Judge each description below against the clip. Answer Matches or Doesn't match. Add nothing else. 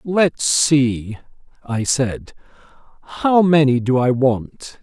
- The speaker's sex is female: Doesn't match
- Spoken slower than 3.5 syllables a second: Matches